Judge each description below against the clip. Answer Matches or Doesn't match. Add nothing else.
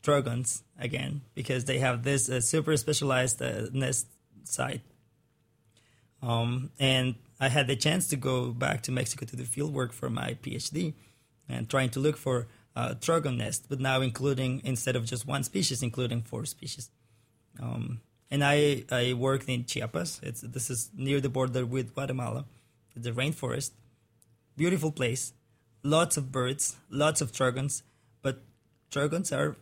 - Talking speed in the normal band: Matches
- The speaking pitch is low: Matches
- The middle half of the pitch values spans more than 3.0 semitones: Doesn't match